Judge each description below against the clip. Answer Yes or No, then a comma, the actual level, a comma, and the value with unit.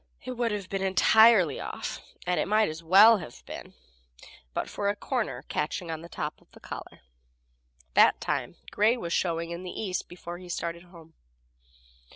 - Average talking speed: Yes, average, 185 wpm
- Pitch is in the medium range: Yes, medium, 180 Hz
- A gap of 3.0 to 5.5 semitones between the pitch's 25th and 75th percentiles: Yes, average, 3.7 semitones